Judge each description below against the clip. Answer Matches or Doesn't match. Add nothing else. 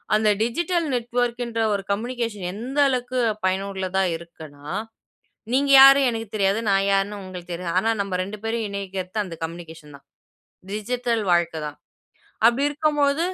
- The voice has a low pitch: Doesn't match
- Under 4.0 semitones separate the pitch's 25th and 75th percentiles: Doesn't match